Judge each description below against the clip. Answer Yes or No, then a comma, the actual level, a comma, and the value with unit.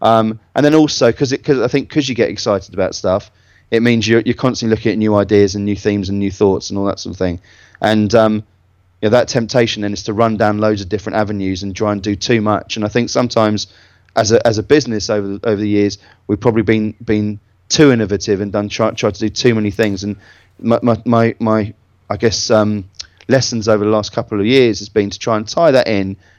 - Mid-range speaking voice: No, low, 105 Hz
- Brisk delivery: Yes, fast, 240 wpm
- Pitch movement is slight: Yes, narrow, 2.1 semitones